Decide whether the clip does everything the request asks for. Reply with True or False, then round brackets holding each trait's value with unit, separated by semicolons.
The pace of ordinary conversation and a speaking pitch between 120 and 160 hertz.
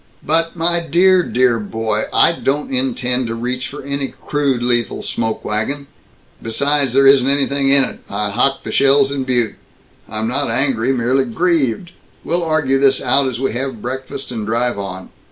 True (175 wpm; 135 Hz)